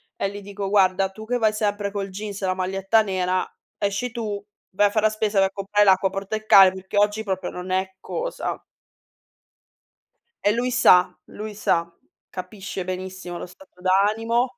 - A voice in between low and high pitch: No, high, 200 Hz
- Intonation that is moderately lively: No, narrow, 2.2 semitones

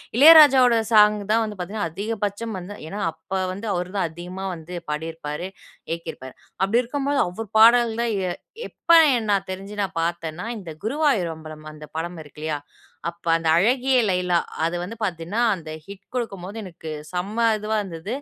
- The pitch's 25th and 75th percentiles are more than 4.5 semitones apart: Yes, average, 5.0 semitones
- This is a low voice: No, high, 190 Hz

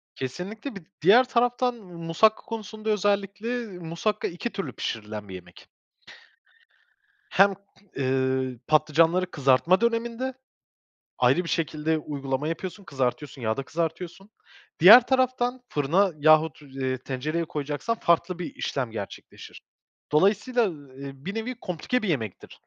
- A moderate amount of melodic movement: No, wide, 7.3 semitones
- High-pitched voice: No, medium, 170 Hz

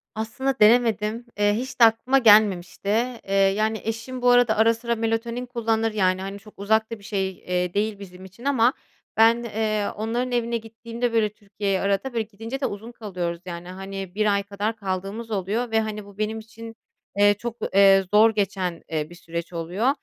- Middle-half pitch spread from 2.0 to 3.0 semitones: Yes, average, 2.7 semitones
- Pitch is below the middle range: No, high, 215 Hz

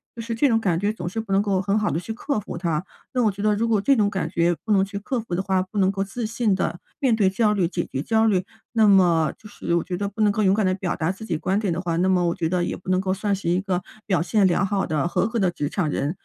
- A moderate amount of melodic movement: Yes, average, 3.1 semitones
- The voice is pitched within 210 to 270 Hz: No, high, 195 Hz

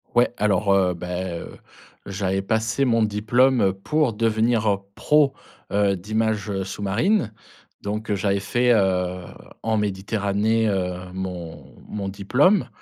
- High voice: No, low, 105 Hz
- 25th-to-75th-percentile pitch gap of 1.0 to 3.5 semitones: Yes, average, 2.8 semitones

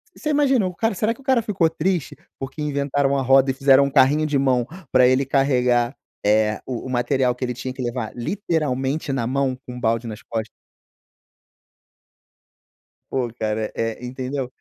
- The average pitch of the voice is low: Yes, low, 130 Hz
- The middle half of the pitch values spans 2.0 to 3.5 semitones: Yes, average, 3.1 semitones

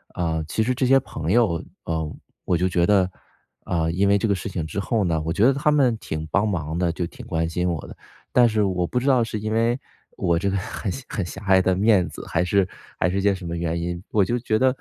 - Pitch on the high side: No, very low, 95 Hz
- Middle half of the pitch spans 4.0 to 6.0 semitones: Yes, average, 4.4 semitones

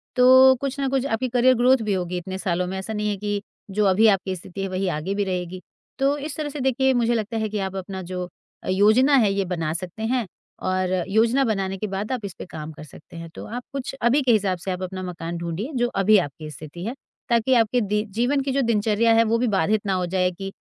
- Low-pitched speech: No, high, 205 Hz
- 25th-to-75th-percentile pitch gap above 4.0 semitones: Yes, average, 4.6 semitones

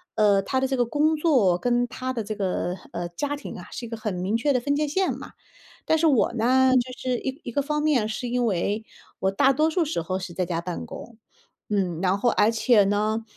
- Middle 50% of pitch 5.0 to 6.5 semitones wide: Yes, average, 5.3 semitones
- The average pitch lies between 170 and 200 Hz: No, high, 235 Hz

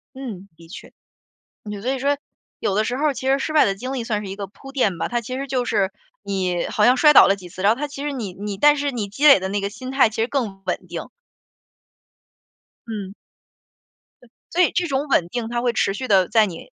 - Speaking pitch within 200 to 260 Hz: Yes, high, 230 Hz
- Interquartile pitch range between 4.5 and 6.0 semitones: Yes, wide, 5.4 semitones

